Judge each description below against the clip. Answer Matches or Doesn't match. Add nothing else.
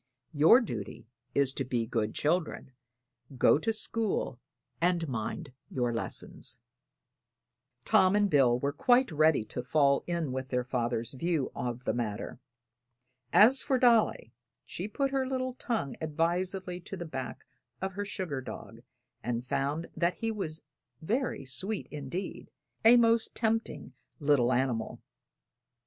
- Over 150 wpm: Doesn't match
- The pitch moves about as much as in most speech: Doesn't match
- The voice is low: Doesn't match